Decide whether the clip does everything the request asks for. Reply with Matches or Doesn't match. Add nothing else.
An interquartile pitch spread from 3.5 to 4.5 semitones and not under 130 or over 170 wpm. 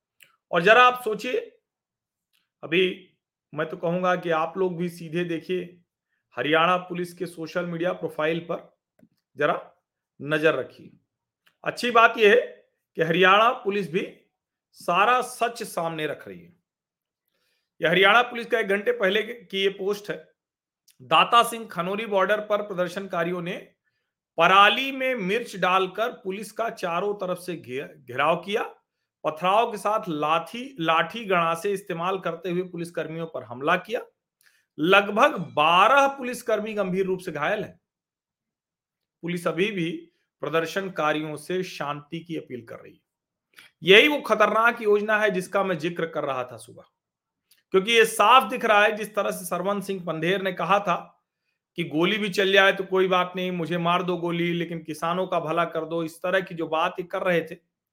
Matches